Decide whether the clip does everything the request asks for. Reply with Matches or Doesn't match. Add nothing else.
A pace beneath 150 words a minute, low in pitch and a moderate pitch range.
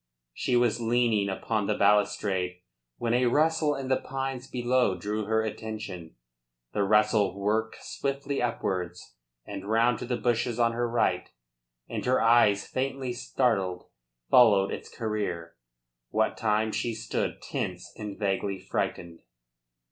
Matches